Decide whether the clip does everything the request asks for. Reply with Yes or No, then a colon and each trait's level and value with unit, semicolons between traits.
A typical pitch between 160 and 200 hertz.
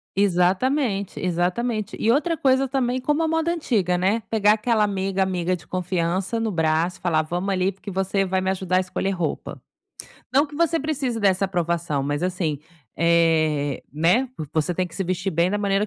Yes: high, 190 Hz